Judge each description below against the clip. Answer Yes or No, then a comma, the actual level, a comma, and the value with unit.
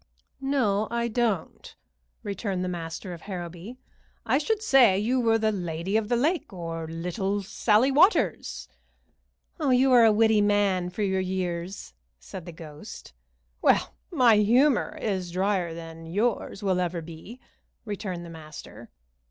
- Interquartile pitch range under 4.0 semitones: No, average, 4.8 semitones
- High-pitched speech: Yes, high, 200 Hz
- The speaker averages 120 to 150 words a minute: Yes, average, 145 wpm